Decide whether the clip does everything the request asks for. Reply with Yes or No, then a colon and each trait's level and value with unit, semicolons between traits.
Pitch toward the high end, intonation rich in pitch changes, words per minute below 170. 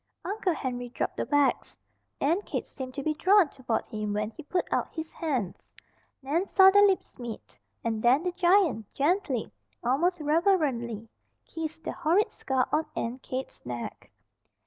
Yes: very high, 295 Hz; wide, 6.3 semitones; average, 160 wpm